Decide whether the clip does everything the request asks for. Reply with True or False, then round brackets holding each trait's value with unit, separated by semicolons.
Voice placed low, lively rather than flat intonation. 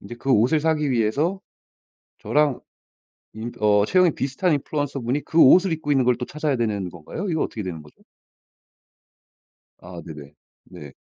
True (130 Hz; 6.5 semitones)